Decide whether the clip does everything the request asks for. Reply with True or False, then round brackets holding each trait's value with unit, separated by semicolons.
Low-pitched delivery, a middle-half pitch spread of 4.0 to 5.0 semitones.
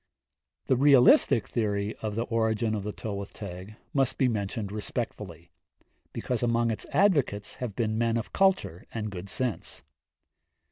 False (110 Hz; 2.9 semitones)